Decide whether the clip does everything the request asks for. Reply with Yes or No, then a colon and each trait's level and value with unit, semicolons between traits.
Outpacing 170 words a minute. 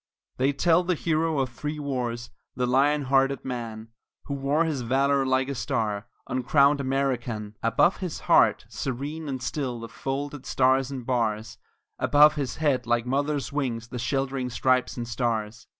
No: average, 160 wpm